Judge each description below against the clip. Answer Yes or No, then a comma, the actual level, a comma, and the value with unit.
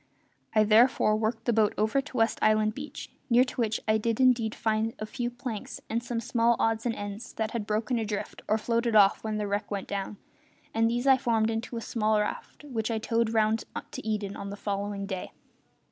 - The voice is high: Yes, high, 220 Hz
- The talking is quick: Yes, fast, 210 wpm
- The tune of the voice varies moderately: No, narrow, 1.7 semitones